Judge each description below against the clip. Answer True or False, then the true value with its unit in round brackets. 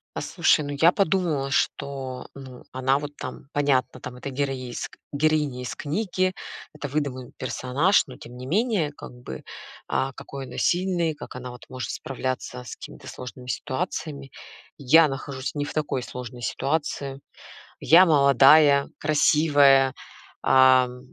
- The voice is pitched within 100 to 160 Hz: True (140 Hz)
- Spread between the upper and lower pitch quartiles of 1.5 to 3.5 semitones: True (2.9 semitones)